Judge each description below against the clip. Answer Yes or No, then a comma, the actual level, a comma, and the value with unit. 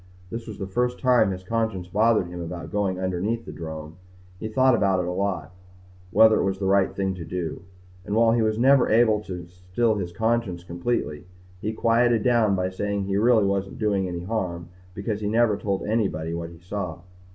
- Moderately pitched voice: No, low, 100 Hz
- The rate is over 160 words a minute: Yes, average, 200 wpm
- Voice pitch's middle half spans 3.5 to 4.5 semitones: Yes, average, 3.8 semitones